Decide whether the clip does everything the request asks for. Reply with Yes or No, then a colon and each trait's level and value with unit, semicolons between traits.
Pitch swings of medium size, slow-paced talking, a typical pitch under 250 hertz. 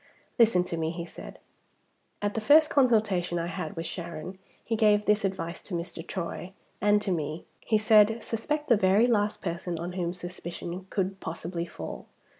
No: average, 3.8 semitones; average, 175 wpm; medium, 185 Hz